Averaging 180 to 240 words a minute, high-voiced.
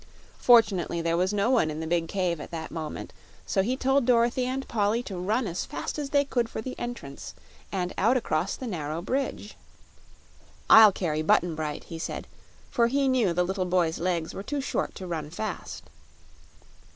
Yes: average, 190 wpm; high, 195 Hz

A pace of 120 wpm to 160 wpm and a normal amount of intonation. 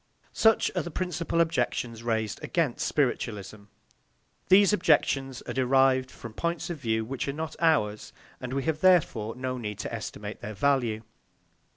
No: average, 155 wpm; wide, 6.2 semitones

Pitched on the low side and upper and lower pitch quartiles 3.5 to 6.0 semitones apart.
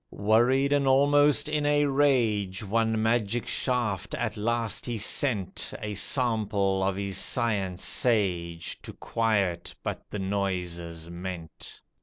Yes: low, 105 Hz; average, 4.4 semitones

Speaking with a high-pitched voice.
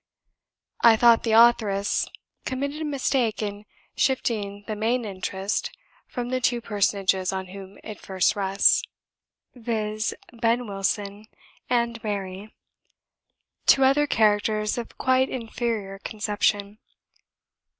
Yes: high, 215 Hz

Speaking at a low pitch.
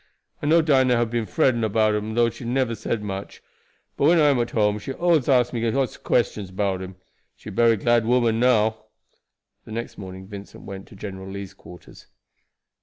Yes: low, 115 Hz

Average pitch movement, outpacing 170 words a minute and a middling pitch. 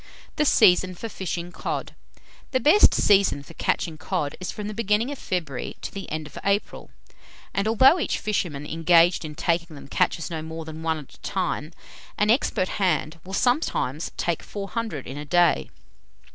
Yes: average, 4.7 semitones; average, 180 wpm; medium, 175 Hz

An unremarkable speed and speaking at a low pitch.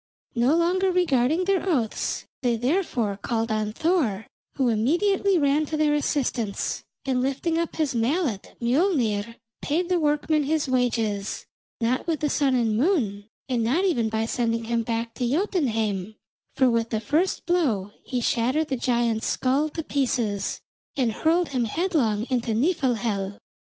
No: average, 150 wpm; very high, 255 Hz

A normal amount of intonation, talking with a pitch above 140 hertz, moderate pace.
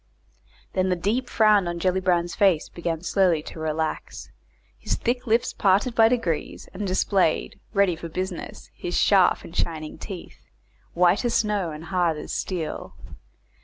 Yes: average, 3.3 semitones; medium, 185 Hz; average, 150 wpm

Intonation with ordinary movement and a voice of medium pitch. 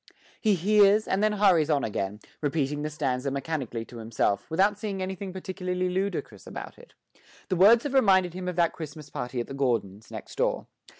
No: wide, 6.3 semitones; medium, 170 Hz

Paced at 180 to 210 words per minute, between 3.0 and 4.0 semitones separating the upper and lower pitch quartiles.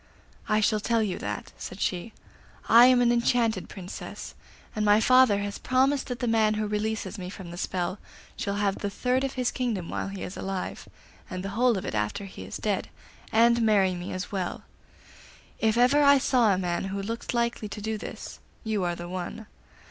Yes: average, 200 wpm; average, 3.7 semitones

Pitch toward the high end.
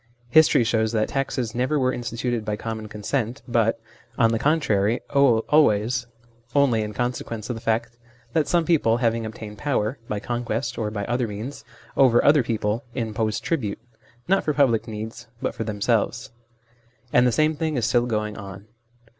No: low, 115 Hz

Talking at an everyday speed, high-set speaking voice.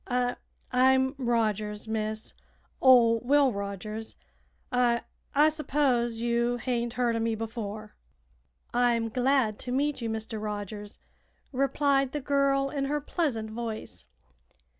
No: slow, 120 wpm; high, 240 Hz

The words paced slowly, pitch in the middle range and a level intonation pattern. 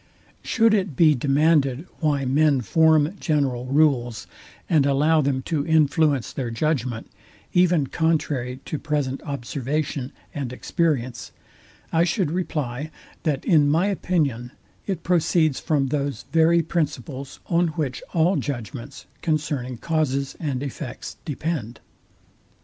No: slow, 120 wpm; medium, 145 Hz; average, 3.5 semitones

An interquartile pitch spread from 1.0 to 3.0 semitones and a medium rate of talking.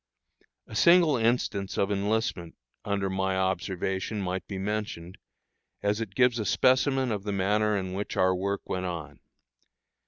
Yes: narrow, 2.5 semitones; average, 150 wpm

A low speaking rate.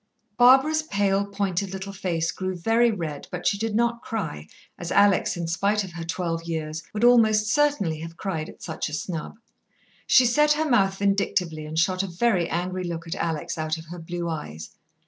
No: average, 190 wpm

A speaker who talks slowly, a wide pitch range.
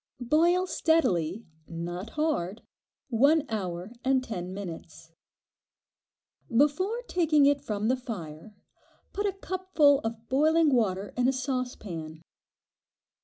Yes: slow, 110 wpm; wide, 8.3 semitones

